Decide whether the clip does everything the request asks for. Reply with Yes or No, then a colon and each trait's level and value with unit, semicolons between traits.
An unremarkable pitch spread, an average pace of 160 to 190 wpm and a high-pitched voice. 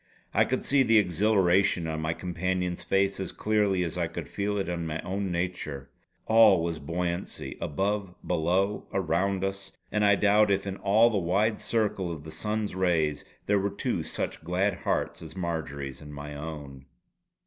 No: average, 3.5 semitones; average, 175 wpm; very low, 95 Hz